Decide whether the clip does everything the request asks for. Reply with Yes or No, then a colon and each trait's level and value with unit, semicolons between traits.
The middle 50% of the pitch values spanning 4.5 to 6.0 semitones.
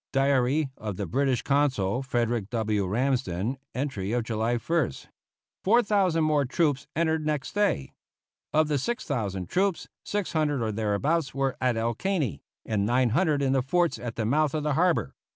Yes: wide, 5.4 semitones